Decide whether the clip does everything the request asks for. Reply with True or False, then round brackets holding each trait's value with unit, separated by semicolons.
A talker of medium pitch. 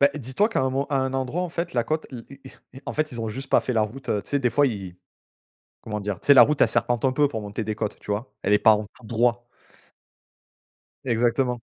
False (125 Hz)